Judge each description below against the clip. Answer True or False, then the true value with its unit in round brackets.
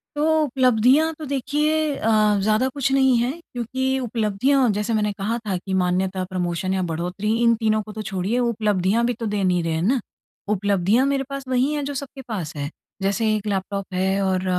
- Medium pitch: False (215 Hz)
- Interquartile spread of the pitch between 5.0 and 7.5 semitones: True (5.3 semitones)